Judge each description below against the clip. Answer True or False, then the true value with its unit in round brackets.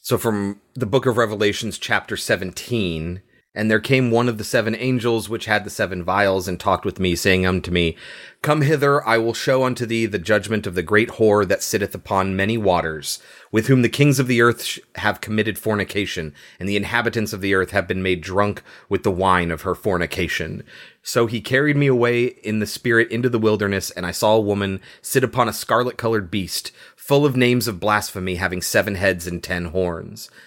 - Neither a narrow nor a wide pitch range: True (3.8 semitones)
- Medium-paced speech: False (210 wpm)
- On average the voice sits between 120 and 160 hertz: False (105 Hz)